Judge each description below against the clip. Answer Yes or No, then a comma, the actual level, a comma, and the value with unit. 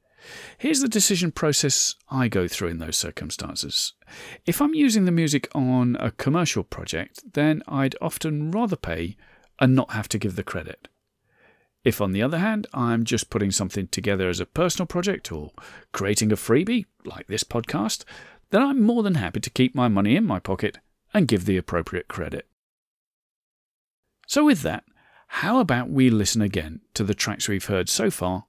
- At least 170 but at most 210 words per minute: Yes, average, 175 wpm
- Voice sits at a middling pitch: No, low, 125 Hz